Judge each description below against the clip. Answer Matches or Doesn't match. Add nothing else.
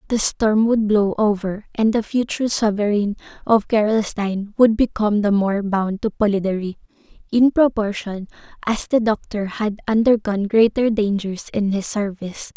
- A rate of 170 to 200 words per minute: Doesn't match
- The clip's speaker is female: Matches